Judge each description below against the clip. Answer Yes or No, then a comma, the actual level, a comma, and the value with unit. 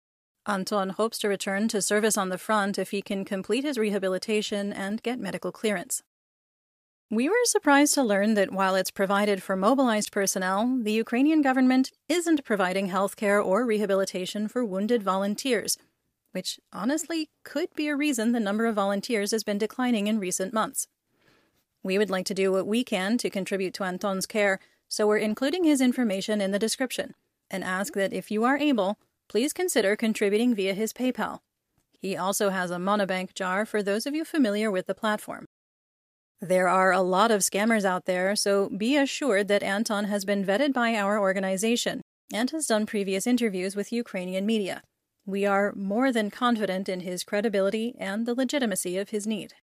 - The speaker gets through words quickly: No, average, 180 wpm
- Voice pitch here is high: Yes, high, 205 Hz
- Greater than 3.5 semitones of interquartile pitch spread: No, average, 3.2 semitones